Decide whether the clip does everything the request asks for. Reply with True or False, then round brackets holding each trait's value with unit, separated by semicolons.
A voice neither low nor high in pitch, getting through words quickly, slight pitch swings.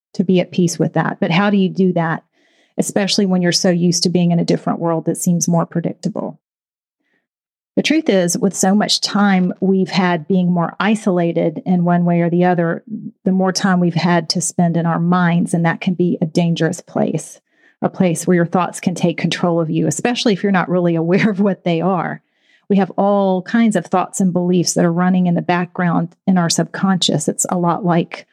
True (180 Hz; 220 wpm; 2.3 semitones)